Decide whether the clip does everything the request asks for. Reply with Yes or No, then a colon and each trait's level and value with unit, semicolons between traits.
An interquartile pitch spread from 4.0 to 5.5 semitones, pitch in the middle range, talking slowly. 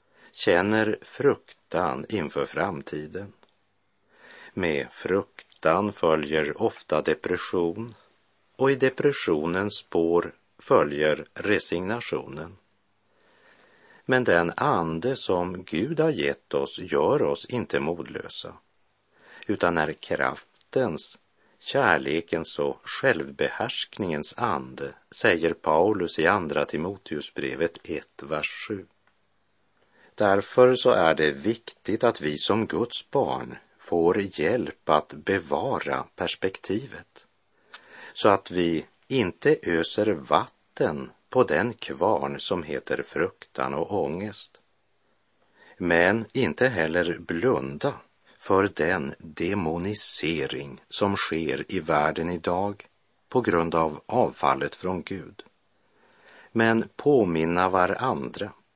No: average, 4.8 semitones; very low, 90 Hz; slow, 95 wpm